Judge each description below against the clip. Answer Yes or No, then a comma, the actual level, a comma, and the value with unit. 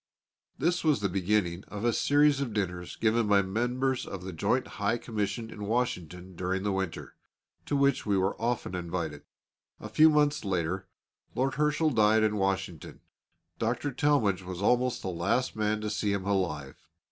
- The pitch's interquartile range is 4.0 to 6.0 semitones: Yes, average, 4.8 semitones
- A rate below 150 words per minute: No, average, 170 wpm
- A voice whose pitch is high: No, low, 105 Hz